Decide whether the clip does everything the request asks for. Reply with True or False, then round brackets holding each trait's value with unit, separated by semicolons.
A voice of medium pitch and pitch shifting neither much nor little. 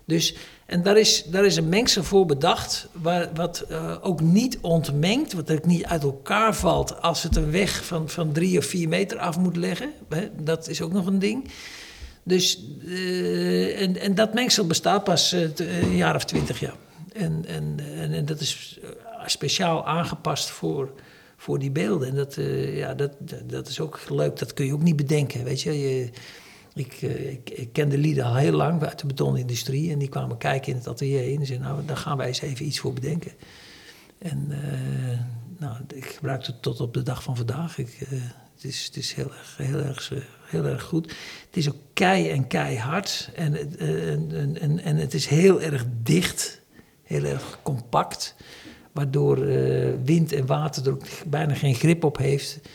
True (150 Hz; 4.0 semitones)